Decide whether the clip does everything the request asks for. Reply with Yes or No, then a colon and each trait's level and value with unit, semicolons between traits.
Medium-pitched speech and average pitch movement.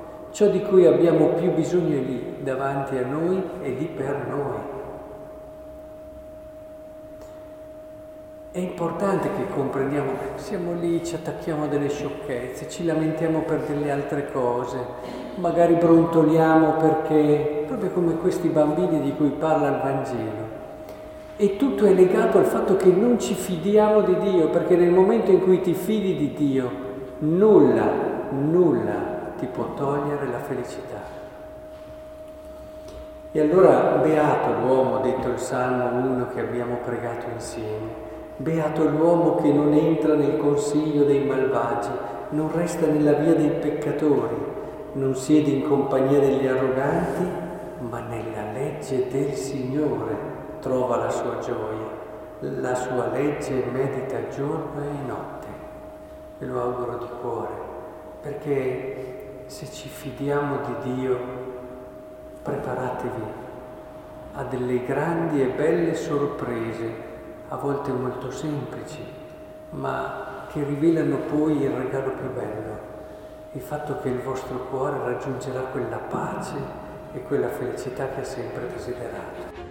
Yes: medium, 150 Hz; average, 4.8 semitones